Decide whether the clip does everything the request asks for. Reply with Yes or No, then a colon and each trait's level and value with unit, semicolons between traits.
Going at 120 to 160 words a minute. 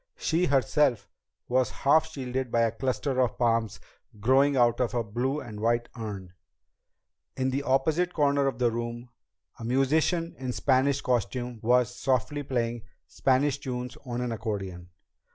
Yes: average, 155 wpm